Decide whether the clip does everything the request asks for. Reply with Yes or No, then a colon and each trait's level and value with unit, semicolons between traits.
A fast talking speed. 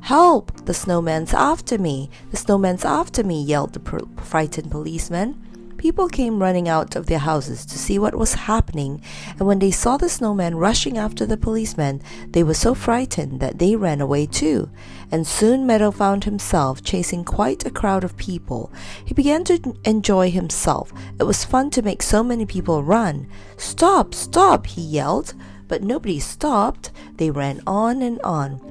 No: average, 170 wpm